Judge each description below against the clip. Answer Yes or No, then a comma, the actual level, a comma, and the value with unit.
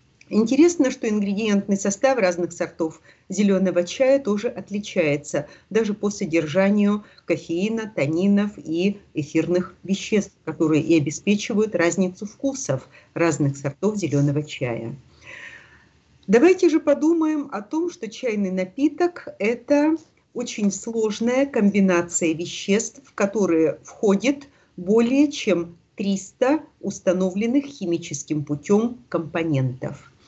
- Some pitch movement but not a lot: No, wide, 5.8 semitones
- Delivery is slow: Yes, slow, 100 wpm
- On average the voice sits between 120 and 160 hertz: No, high, 200 Hz